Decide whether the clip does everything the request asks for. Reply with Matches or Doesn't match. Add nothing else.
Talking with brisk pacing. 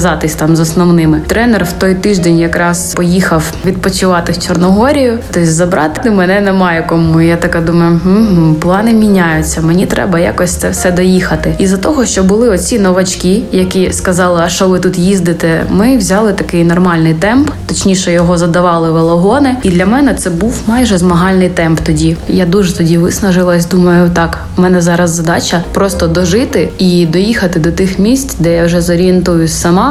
Matches